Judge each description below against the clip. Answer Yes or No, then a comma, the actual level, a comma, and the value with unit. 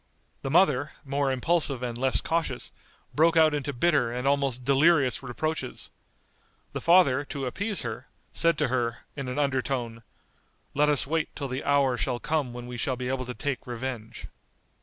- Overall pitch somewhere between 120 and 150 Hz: Yes, low, 135 Hz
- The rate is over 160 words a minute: Yes, average, 175 wpm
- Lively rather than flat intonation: No, average, 3.0 semitones